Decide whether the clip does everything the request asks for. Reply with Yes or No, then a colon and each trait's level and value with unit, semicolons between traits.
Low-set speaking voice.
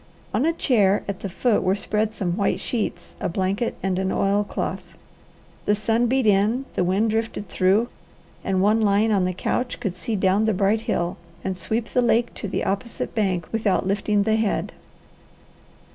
No: high, 205 Hz